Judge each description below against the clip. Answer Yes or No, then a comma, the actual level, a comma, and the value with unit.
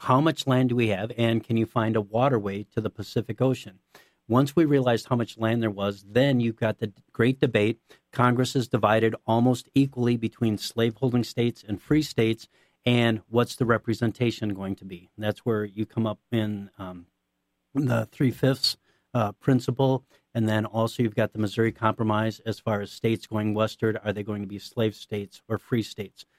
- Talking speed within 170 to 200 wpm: Yes, average, 190 wpm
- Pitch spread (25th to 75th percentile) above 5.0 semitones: No, narrow, 2.4 semitones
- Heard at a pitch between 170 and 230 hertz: No, low, 115 Hz